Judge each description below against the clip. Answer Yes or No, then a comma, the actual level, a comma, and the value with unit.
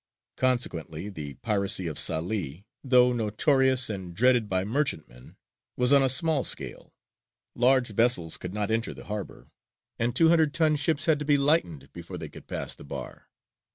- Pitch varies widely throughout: Yes, wide, 6.7 semitones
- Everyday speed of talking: Yes, average, 165 wpm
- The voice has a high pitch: No, low, 115 Hz